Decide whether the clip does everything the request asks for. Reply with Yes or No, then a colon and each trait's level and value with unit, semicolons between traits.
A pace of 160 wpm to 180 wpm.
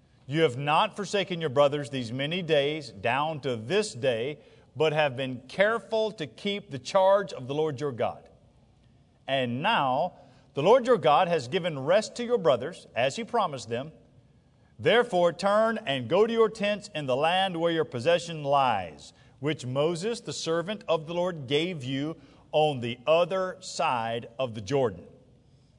Yes: average, 170 wpm